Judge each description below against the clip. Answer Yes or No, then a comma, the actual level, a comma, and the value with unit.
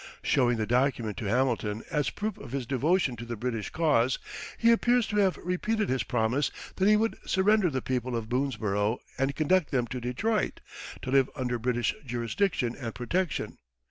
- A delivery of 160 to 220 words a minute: Yes, average, 175 wpm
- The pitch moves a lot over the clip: Yes, wide, 7.3 semitones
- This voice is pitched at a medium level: No, low, 130 Hz